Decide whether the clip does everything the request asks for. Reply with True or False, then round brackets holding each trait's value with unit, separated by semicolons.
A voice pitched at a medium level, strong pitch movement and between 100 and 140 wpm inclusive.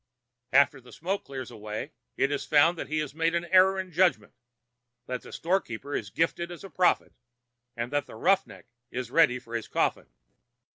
False (150 Hz; 5.7 semitones; 185 wpm)